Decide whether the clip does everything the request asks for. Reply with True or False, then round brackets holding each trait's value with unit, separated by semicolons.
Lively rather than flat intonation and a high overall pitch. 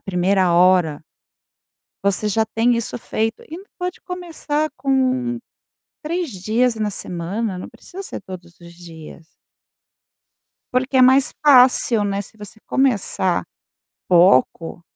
True (6.2 semitones; 220 Hz)